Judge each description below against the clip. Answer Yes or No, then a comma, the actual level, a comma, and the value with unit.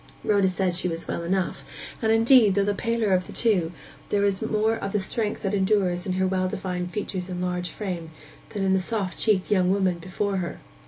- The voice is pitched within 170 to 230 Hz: Yes, high, 190 Hz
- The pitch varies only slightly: Yes, narrow, 2.3 semitones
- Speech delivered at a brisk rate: Yes, fast, 215 wpm